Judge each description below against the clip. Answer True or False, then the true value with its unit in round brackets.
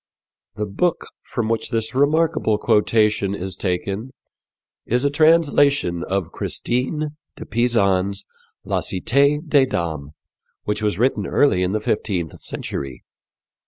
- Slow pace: True (125 wpm)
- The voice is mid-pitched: False (110 Hz)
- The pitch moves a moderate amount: False (6.5 semitones)